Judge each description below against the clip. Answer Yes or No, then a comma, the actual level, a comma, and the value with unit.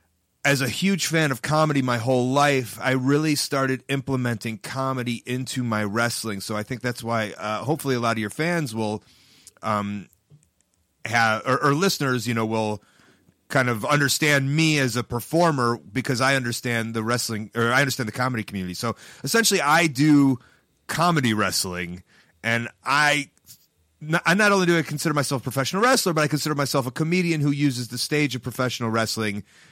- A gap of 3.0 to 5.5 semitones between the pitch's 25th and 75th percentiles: Yes, average, 4.6 semitones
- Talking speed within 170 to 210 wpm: Yes, average, 180 wpm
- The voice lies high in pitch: No, low, 130 Hz